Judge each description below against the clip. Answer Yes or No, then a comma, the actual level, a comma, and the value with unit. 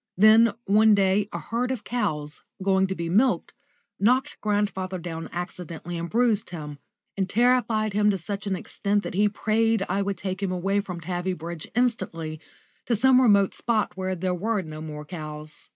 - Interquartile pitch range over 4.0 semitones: No, average, 3.7 semitones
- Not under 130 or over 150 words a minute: No, average, 175 wpm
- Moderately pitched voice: No, high, 195 Hz